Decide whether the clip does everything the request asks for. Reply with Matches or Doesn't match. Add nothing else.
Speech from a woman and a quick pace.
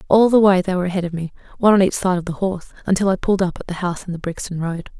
Matches